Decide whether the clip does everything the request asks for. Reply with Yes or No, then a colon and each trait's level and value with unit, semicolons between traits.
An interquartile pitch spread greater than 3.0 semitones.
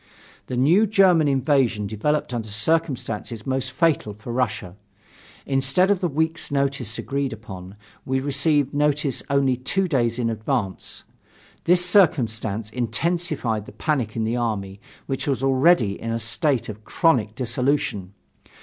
Yes: average, 5.0 semitones